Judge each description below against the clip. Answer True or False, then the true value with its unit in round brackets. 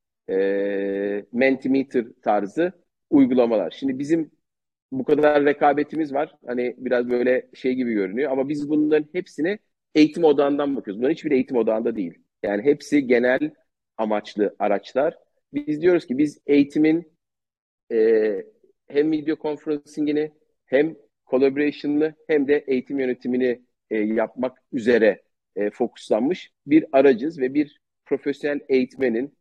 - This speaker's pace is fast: False (120 wpm)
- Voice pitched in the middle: True (145 Hz)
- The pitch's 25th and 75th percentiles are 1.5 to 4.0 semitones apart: True (3.7 semitones)